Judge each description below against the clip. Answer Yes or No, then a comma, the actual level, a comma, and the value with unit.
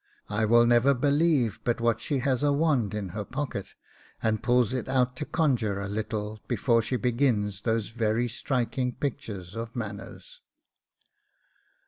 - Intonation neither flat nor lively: Yes, average, 3.4 semitones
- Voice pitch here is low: Yes, low, 120 Hz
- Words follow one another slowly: No, average, 150 wpm